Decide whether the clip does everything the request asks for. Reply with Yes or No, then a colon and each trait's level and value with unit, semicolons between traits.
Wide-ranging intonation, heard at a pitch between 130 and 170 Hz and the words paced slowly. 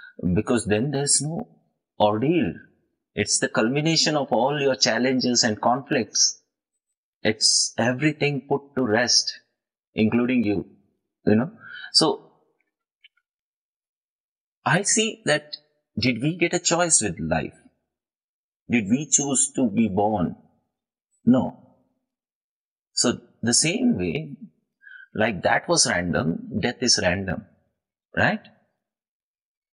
Yes: wide, 7.6 semitones; low, 135 Hz; slow, 105 wpm